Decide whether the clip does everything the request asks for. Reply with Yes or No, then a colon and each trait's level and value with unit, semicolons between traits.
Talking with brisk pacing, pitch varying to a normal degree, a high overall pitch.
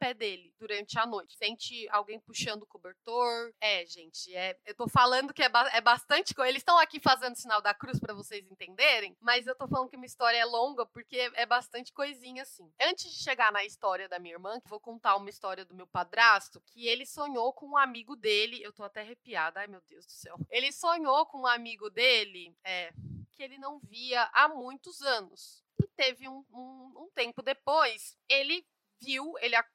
Yes: fast, 210 wpm; average, 4.1 semitones; high, 235 Hz